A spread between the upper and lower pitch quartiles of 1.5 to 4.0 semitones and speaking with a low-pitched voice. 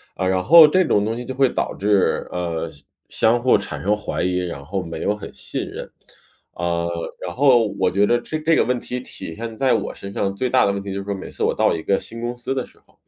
No: average, 4.8 semitones; low, 105 Hz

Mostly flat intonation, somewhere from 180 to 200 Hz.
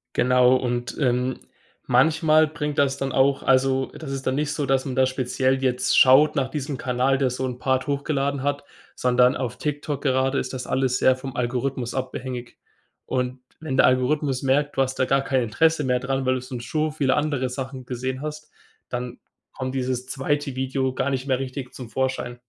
No: narrow, 1.6 semitones; low, 130 Hz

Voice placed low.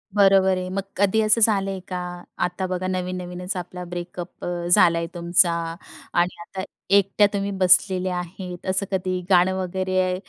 No: medium, 185 Hz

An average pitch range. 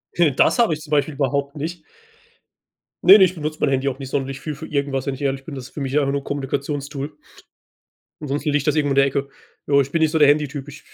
No: narrow, 1.8 semitones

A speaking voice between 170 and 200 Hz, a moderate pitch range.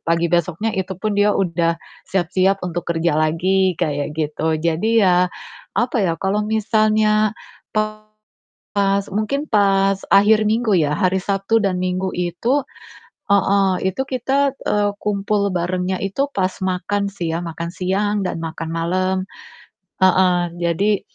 Yes: high, 190 Hz; average, 3.0 semitones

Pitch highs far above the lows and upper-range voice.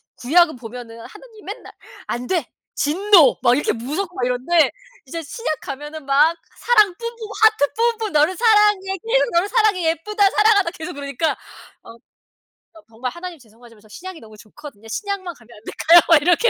Yes: wide, 7.8 semitones; very high, 330 Hz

